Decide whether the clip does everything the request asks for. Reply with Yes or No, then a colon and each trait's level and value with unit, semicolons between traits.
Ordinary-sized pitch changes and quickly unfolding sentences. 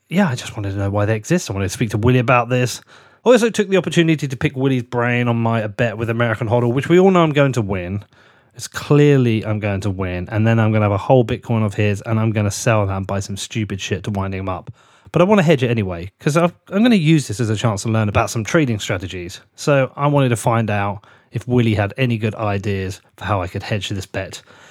Yes: average, 4.4 semitones; fast, 275 wpm